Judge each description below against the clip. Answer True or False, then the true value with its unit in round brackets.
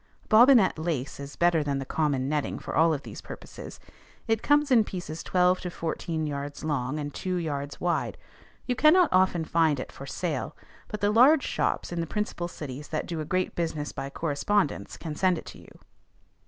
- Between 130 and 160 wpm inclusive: False (195 wpm)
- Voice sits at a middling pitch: True (165 Hz)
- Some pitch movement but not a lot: True (4.1 semitones)